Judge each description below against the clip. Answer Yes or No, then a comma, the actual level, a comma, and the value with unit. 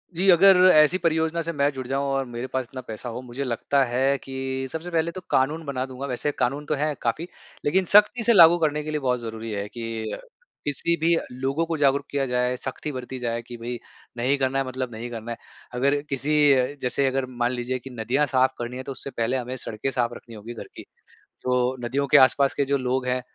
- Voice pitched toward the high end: No, low, 130 Hz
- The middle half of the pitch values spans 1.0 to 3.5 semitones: Yes, average, 3.0 semitones